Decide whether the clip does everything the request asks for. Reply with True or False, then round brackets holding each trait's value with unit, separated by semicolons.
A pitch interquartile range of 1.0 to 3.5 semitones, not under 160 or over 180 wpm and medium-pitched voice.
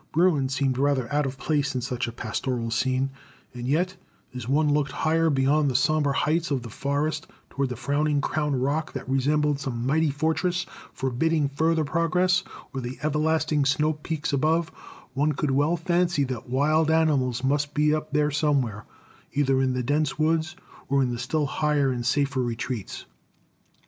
True (2.9 semitones; 170 wpm; 145 Hz)